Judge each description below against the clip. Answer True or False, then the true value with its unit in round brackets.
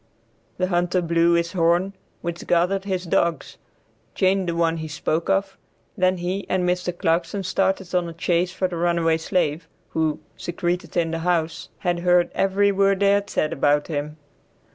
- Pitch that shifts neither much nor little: False (1.9 semitones)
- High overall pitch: False (175 Hz)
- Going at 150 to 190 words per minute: True (170 wpm)